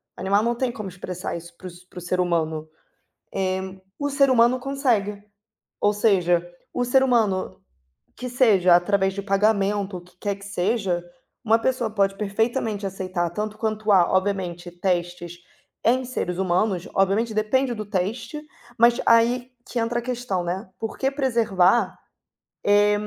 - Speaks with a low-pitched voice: No, high, 200 Hz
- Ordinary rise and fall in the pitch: Yes, average, 4.3 semitones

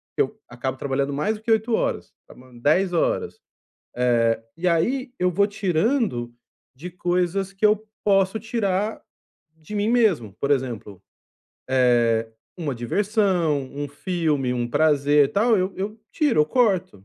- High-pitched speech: No, medium, 175 Hz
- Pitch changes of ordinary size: No, wide, 7.0 semitones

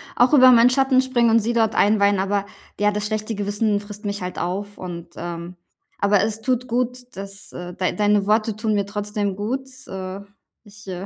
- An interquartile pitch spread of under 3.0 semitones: Yes, narrow, 2.5 semitones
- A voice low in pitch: No, high, 205 Hz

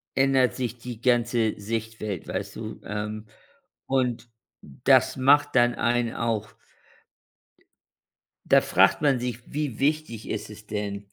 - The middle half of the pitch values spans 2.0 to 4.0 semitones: Yes, average, 2.9 semitones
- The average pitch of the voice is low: Yes, low, 115 Hz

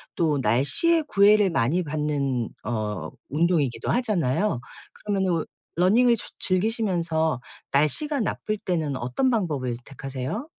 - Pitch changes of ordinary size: No, wide, 7.4 semitones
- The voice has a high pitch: No, medium, 165 Hz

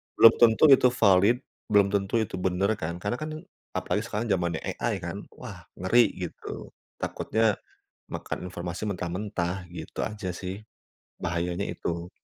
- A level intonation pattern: No, average, 3.5 semitones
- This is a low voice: Yes, very low, 95 Hz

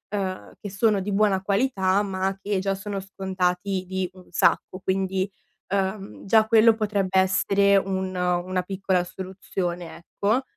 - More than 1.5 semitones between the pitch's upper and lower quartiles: No, narrow, 1.2 semitones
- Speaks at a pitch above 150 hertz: Yes, high, 190 Hz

